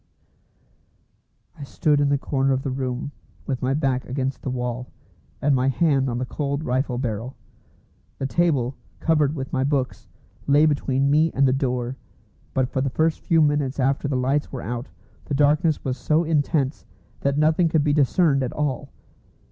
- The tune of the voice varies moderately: No, narrow, 2.3 semitones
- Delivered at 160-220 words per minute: Yes, average, 175 wpm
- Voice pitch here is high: No, low, 135 Hz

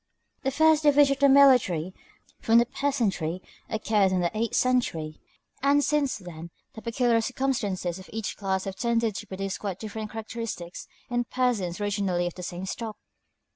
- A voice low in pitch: No, high, 220 Hz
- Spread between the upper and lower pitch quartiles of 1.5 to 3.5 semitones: No, average, 5.2 semitones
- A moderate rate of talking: Yes, average, 165 wpm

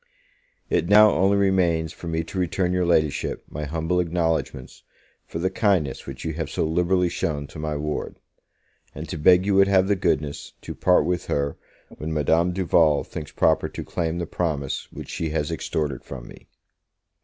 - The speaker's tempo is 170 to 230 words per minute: Yes, average, 180 wpm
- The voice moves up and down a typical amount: Yes, average, 3.0 semitones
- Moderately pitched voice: No, very low, 80 Hz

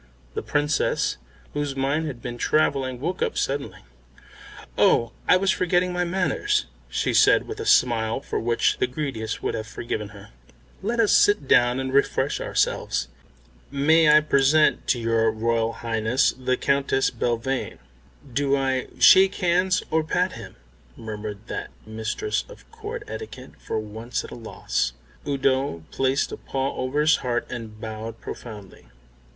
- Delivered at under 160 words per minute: Yes, average, 150 wpm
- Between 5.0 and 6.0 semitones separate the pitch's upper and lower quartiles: Yes, average, 5.3 semitones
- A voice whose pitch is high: No, low, 135 Hz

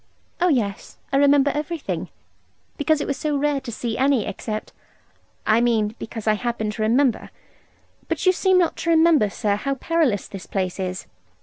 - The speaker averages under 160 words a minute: No, average, 175 wpm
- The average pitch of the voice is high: Yes, very high, 255 Hz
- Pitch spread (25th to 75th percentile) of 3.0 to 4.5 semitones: No, wide, 5.6 semitones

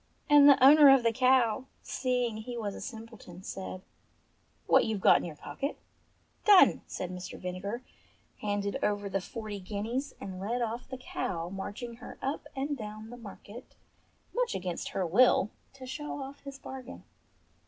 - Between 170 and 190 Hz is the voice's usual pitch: No, high, 230 Hz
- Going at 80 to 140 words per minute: No, average, 165 wpm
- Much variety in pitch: No, average, 4.7 semitones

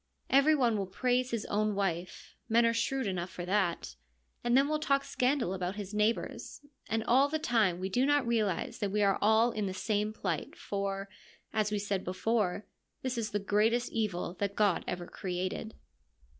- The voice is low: No, high, 210 Hz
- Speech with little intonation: No, average, 3.6 semitones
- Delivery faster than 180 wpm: Yes, average, 195 wpm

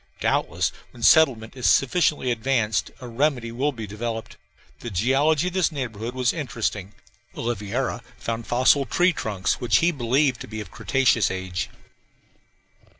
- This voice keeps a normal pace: Yes, average, 145 wpm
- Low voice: Yes, low, 120 Hz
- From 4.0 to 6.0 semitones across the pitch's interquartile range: No, average, 3.6 semitones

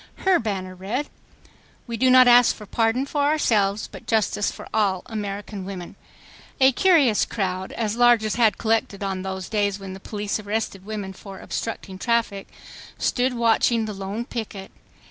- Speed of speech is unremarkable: Yes, average, 160 wpm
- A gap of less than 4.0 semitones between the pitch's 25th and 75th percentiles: Yes, average, 3.3 semitones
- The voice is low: No, high, 215 Hz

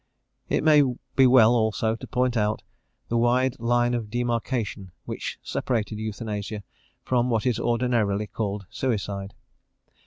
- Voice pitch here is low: Yes, low, 115 Hz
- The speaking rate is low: Yes, slow, 130 wpm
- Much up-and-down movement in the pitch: No, narrow, 2.5 semitones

